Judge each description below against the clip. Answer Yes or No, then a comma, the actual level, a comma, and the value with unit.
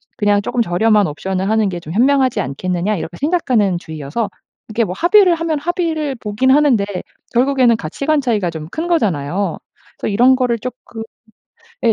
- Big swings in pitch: Yes, wide, 6.5 semitones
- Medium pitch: No, high, 225 Hz